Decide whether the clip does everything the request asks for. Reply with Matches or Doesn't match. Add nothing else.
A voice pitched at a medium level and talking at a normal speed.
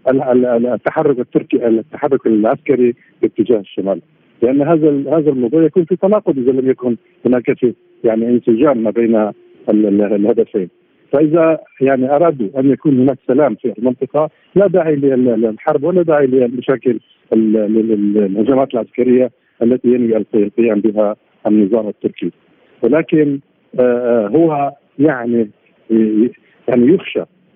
Doesn't match